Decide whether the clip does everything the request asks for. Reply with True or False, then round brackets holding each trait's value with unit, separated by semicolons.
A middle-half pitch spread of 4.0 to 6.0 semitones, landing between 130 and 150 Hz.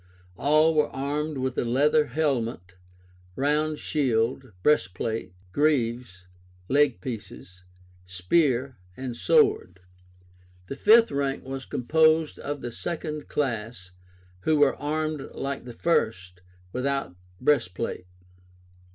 True (4.6 semitones; 135 Hz)